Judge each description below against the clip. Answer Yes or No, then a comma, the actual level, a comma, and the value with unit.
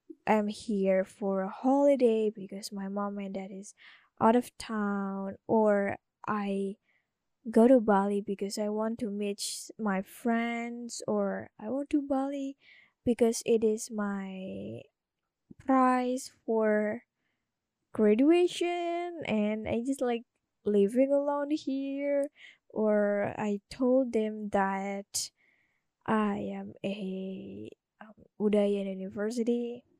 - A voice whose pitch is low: No, high, 215 Hz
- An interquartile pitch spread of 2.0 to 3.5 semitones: No, average, 3.9 semitones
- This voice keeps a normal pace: No, slow, 110 wpm